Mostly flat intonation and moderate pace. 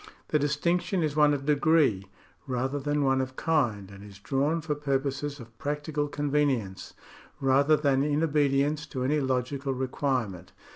Yes: narrow, 2.2 semitones; average, 150 wpm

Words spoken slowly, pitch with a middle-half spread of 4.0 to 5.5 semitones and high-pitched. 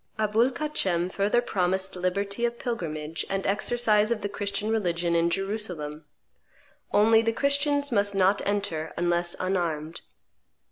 Yes: slow, 130 wpm; average, 4.3 semitones; high, 200 Hz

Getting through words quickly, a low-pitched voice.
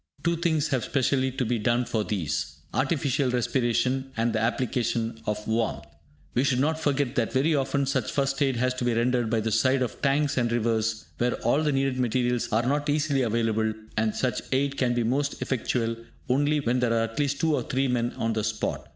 Yes: fast, 210 wpm; low, 125 Hz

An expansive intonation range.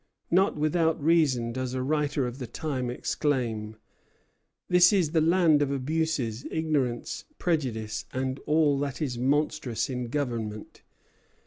No: average, 4.1 semitones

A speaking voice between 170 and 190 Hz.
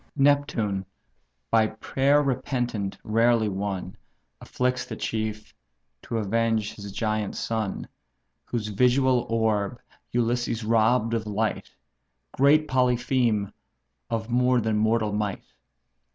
No: low, 115 Hz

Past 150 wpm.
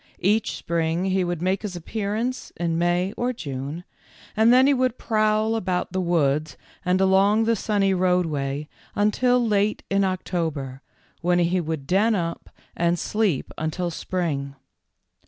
No: average, 145 wpm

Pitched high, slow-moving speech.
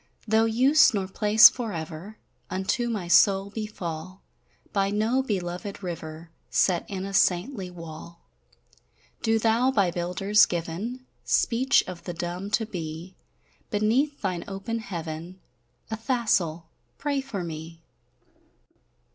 Yes: high, 195 Hz; slow, 115 wpm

